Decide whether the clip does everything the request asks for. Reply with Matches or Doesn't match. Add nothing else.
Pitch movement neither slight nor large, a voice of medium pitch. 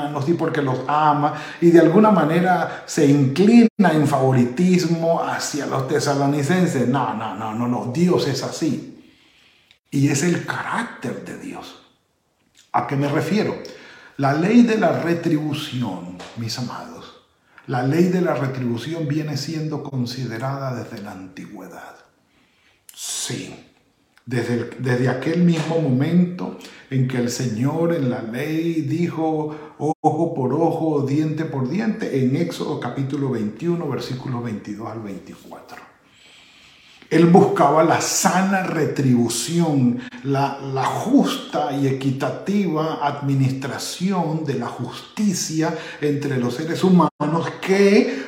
Matches